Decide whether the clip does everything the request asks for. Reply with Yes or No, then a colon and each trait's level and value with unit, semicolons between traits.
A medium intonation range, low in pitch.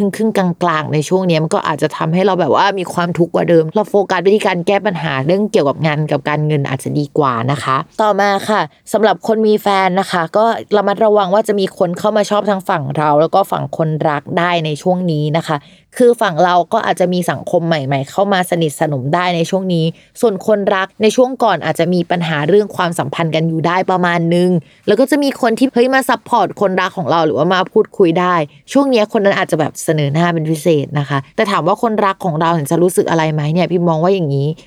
No: average, 4.0 semitones; medium, 180 Hz